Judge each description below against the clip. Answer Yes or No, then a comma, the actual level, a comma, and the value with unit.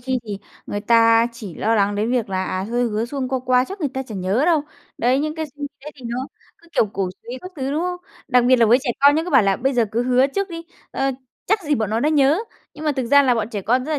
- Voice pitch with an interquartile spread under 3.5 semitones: No, average, 4.1 semitones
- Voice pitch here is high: Yes, very high, 255 Hz